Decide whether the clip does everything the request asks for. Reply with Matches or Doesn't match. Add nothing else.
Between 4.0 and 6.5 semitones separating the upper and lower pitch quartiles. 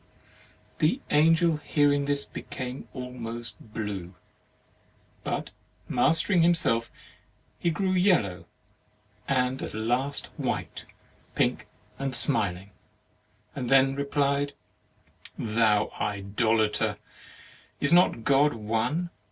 Matches